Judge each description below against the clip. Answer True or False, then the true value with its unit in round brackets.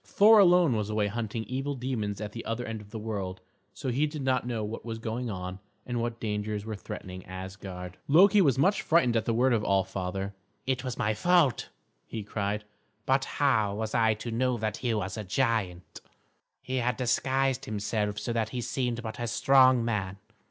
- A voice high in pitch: False (115 Hz)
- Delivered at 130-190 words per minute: False (200 wpm)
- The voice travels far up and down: False (3.7 semitones)